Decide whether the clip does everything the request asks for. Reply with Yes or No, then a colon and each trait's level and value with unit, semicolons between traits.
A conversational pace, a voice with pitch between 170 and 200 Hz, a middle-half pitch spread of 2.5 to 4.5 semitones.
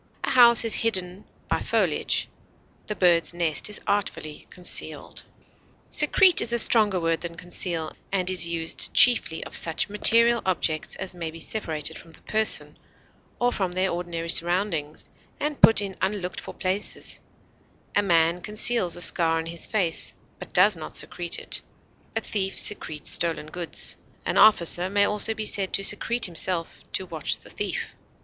Yes: average, 160 wpm; medium, 185 Hz; average, 3.8 semitones